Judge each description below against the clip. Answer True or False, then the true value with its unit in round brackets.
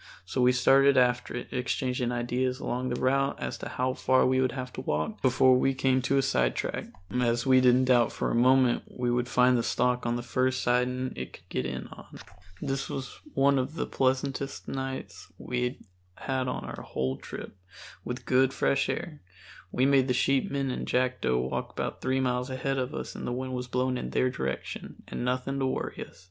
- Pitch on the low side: True (130 Hz)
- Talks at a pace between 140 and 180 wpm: False (205 wpm)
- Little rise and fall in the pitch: True (1.1 semitones)